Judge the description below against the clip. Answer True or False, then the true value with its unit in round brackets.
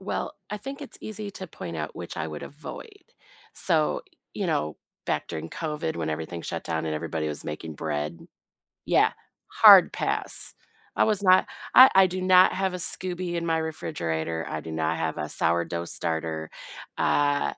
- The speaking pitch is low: True (85 Hz)